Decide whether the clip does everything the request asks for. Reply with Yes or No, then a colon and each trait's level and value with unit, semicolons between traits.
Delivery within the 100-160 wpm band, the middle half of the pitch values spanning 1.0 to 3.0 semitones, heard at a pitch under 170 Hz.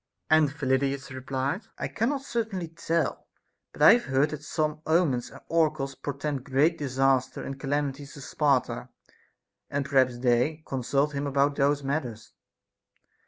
Yes: average, 145 wpm; narrow, 2.5 semitones; medium, 140 Hz